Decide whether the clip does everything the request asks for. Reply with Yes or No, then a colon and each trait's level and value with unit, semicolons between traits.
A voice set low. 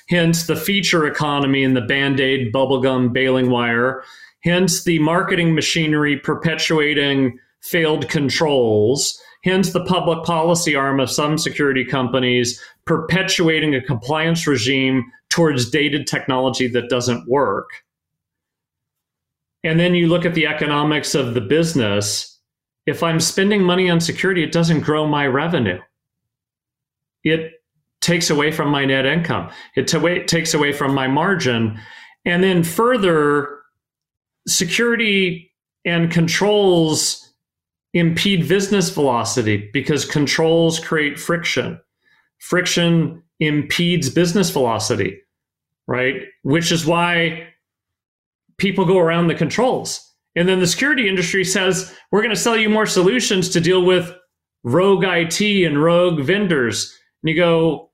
No: medium, 160 Hz